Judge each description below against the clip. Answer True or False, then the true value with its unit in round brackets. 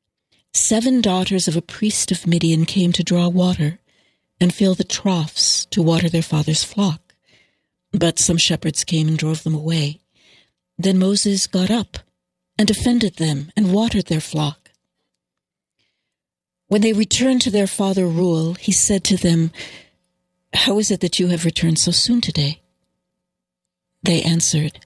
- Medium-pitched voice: True (175 Hz)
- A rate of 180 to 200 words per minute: False (150 wpm)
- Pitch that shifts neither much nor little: True (3.5 semitones)